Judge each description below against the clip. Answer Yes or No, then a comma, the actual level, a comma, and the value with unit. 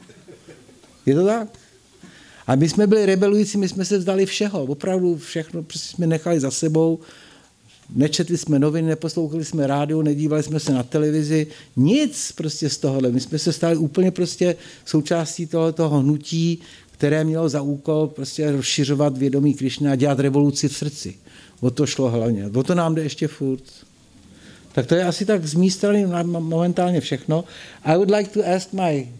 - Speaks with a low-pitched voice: No, medium, 160 Hz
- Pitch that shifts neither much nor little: Yes, average, 3.2 semitones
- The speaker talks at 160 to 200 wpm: Yes, fast, 170 wpm